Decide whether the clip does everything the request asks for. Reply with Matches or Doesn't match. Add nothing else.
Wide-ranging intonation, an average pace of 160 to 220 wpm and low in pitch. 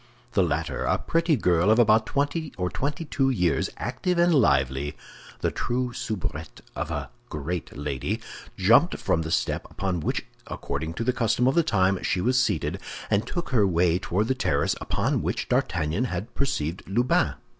Matches